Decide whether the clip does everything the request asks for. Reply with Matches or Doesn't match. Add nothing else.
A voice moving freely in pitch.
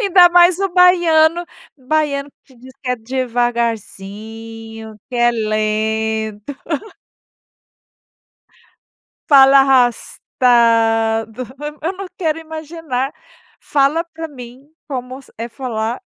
Matches